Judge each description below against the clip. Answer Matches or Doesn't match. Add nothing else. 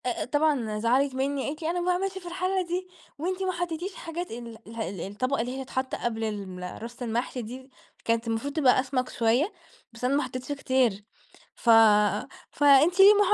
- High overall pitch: Matches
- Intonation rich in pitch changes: Matches